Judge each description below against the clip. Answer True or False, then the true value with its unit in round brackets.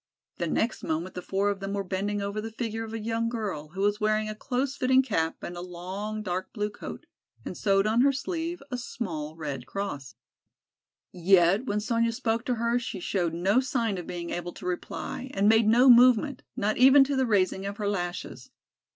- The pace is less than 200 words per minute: False (205 wpm)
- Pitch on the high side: True (210 Hz)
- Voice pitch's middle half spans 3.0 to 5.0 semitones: True (4.1 semitones)